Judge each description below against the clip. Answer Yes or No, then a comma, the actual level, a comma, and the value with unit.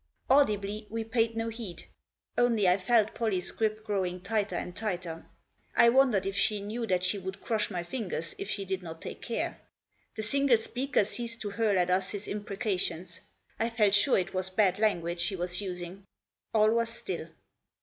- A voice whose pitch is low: No, high, 205 Hz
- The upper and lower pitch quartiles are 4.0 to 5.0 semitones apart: No, average, 3.4 semitones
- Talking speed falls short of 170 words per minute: No, average, 185 wpm